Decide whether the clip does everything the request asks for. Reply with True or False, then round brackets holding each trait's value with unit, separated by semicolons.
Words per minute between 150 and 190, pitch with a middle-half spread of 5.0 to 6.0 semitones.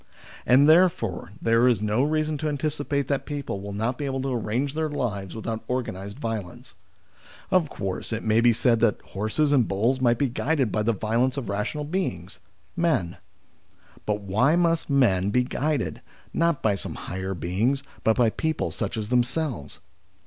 True (175 wpm; 5.5 semitones)